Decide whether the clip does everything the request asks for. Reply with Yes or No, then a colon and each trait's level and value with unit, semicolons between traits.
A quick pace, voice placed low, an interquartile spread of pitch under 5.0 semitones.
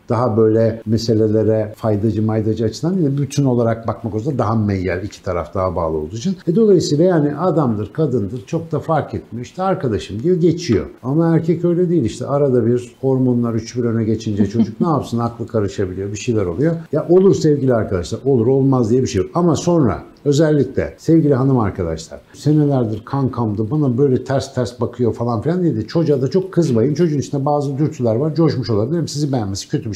No: fast, 190 wpm; low, 125 Hz; wide, 5.6 semitones